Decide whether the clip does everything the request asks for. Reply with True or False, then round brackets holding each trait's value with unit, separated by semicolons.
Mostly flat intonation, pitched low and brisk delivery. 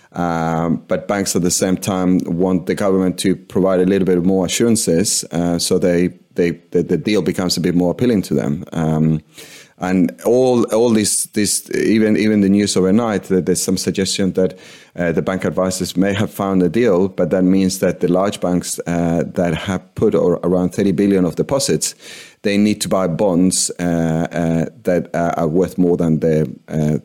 False (2.3 semitones; 90 Hz; 195 wpm)